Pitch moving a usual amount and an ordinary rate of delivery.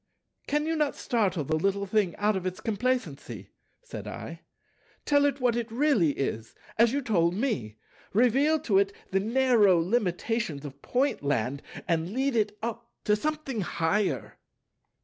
No: wide, 6.4 semitones; average, 150 wpm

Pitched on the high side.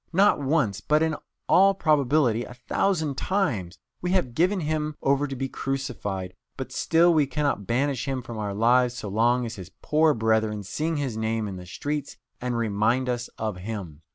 No: low, 125 Hz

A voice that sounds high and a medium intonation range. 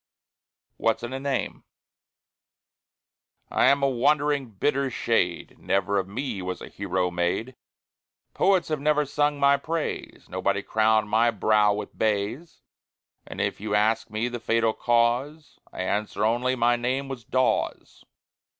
No: low, 120 Hz; average, 4.6 semitones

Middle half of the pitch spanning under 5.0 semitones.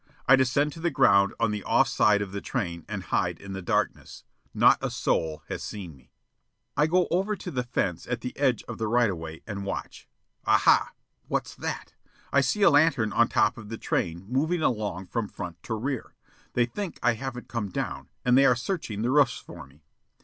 No: wide, 5.4 semitones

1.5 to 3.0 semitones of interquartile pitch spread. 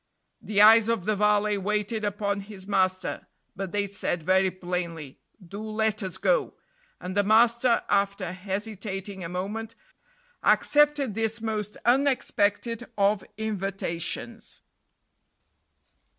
Yes: narrow, 2.4 semitones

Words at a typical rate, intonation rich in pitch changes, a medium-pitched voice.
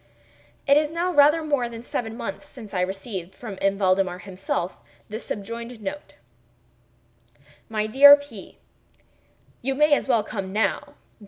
No: average, 145 wpm; wide, 6.5 semitones; high, 225 Hz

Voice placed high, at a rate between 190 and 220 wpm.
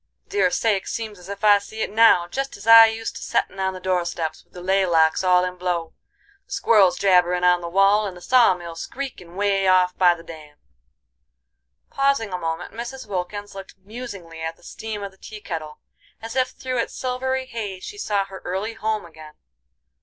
Yes: high, 195 Hz; average, 200 wpm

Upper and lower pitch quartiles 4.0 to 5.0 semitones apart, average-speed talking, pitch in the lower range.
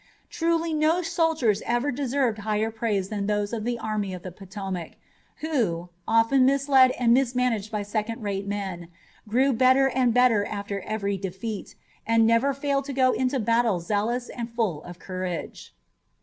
No: average, 4.3 semitones; average, 160 wpm; high, 225 Hz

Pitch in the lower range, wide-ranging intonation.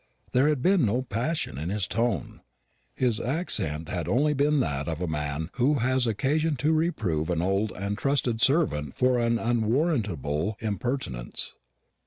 Yes: low, 115 Hz; wide, 7.8 semitones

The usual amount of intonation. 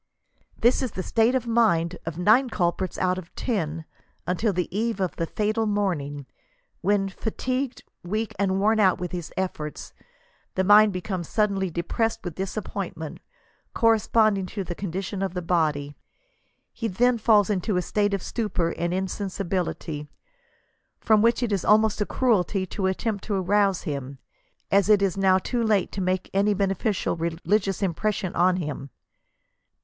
Yes: average, 3.2 semitones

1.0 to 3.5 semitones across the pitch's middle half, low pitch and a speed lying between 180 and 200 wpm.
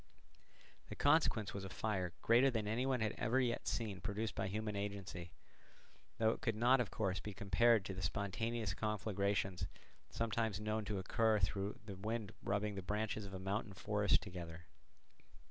No: narrow, 2.4 semitones; low, 105 Hz; average, 170 wpm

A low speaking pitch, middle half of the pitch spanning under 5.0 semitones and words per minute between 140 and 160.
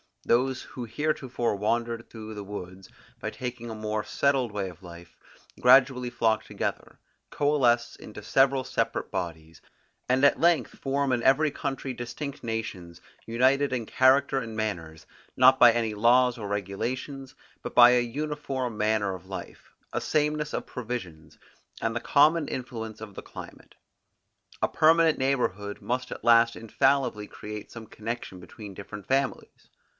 Yes: low, 120 Hz; average, 3.9 semitones; average, 150 wpm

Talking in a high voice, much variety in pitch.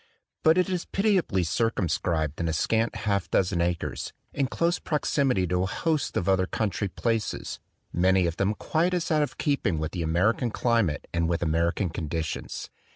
No: very low, 95 Hz; wide, 8.0 semitones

